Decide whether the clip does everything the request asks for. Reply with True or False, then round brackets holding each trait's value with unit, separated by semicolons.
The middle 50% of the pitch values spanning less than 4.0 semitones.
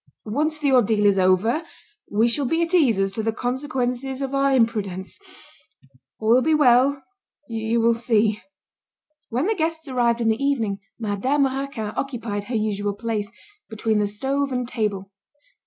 False (4.3 semitones)